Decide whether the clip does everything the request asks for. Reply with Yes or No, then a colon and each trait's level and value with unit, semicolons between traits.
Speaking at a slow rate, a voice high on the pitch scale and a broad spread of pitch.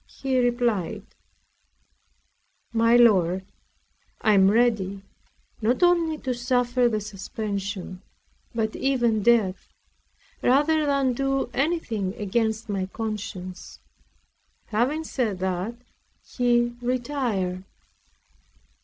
No: slow, 90 wpm; high, 230 Hz; average, 4.0 semitones